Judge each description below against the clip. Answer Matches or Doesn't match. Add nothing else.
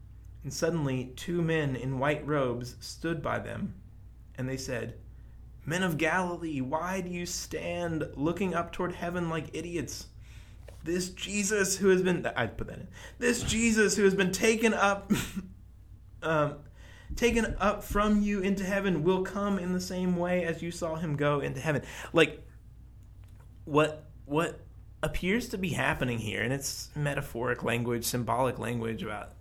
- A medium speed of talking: Matches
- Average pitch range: Doesn't match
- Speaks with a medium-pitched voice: Matches